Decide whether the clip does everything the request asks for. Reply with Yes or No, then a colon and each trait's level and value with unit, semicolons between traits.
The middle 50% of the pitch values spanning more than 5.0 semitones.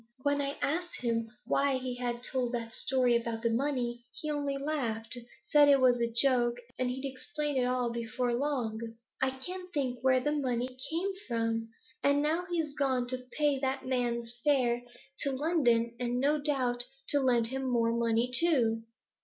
No: average, 3.1 semitones